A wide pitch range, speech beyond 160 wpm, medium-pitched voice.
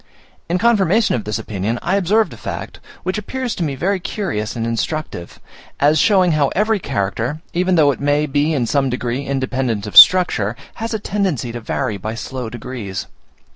Yes: wide, 7.9 semitones; average, 180 wpm; medium, 145 Hz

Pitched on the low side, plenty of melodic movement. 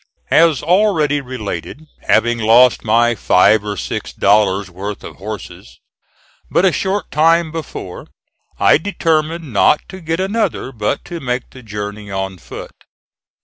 Yes: low, 125 Hz; wide, 7.9 semitones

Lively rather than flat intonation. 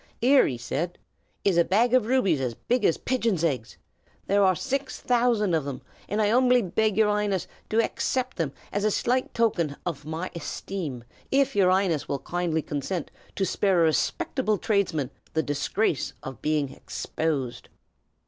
Yes: wide, 6.1 semitones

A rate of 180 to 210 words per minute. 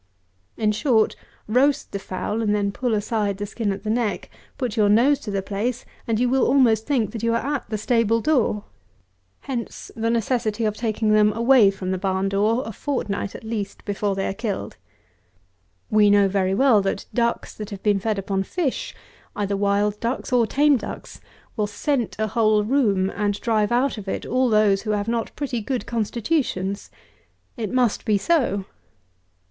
Yes: average, 185 wpm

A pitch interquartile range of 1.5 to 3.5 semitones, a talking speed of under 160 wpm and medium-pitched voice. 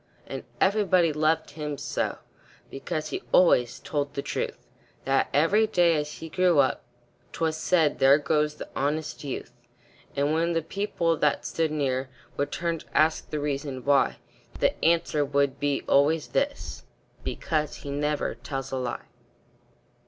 Yes: average, 2.7 semitones; average, 150 wpm; medium, 150 Hz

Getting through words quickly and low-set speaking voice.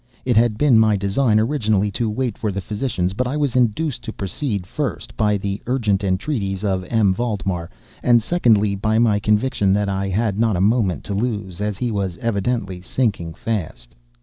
No: average, 185 wpm; low, 105 Hz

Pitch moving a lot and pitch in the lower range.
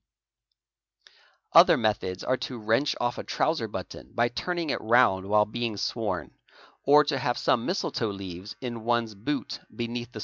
No: average, 3.1 semitones; low, 120 Hz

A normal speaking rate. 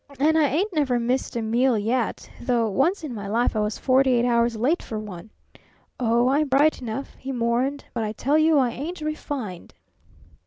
Yes: average, 195 wpm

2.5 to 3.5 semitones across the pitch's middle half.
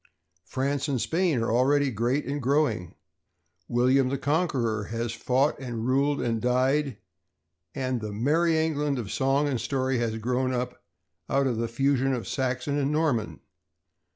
Yes: average, 3.1 semitones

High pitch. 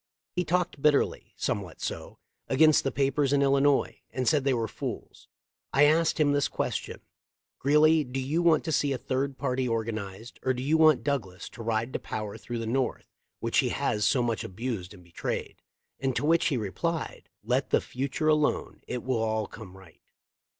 No: low, 130 Hz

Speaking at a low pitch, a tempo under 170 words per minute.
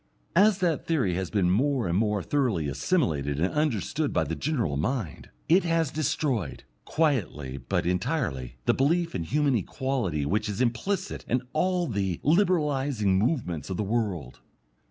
Yes: low, 115 Hz; average, 155 wpm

